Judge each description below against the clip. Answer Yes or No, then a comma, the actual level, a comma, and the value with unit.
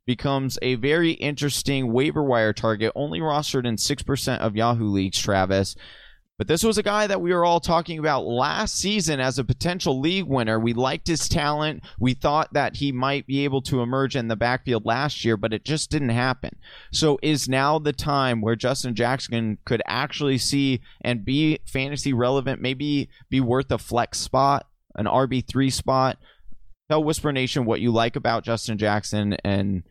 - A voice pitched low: Yes, low, 130 Hz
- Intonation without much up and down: No, average, 3.8 semitones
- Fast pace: No, average, 180 wpm